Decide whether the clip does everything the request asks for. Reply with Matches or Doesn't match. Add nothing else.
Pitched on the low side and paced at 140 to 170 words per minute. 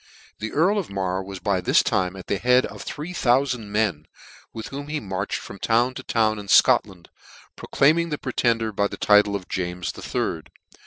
Doesn't match